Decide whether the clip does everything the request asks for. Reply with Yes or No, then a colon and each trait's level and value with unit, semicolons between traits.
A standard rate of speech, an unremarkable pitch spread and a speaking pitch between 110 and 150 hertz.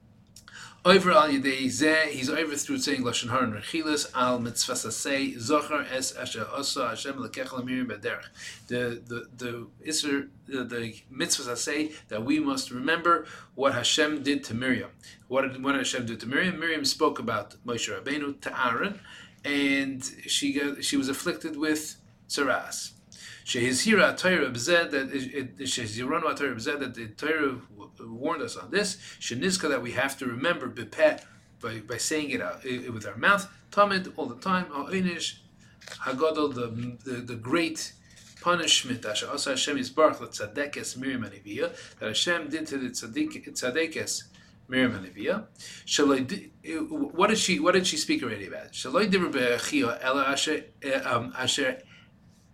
Yes: average, 165 wpm; average, 5.0 semitones; medium, 140 Hz